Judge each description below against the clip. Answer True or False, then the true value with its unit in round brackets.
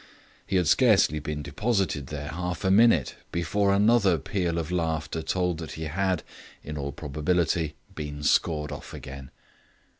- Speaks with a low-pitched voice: True (80 Hz)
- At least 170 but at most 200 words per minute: False (150 wpm)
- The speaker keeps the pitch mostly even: False (3.6 semitones)